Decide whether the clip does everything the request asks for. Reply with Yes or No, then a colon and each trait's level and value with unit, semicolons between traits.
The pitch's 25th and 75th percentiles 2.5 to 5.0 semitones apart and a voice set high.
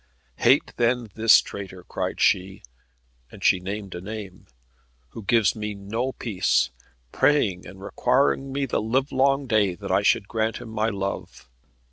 No: average, 3.9 semitones; low, 110 Hz